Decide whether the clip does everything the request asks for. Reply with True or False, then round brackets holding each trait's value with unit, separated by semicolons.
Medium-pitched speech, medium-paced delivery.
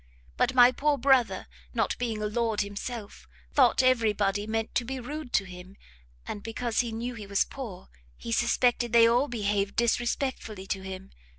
False (230 Hz; 175 wpm)